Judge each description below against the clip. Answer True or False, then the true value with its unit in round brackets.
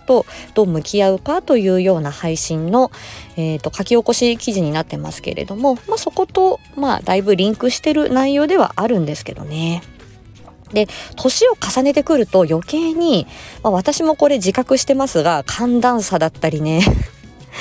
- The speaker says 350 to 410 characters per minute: False (330 characters per minute)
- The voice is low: False (230 Hz)